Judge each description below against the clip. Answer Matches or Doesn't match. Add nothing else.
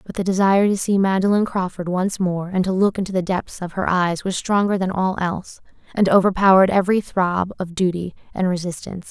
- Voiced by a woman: Matches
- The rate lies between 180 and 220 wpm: Matches